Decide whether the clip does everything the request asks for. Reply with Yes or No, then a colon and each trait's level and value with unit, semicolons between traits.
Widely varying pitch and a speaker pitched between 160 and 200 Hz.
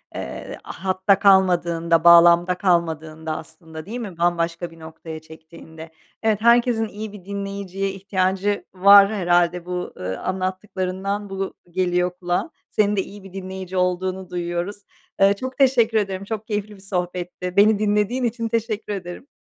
No: average, 2.8 semitones; high, 190 Hz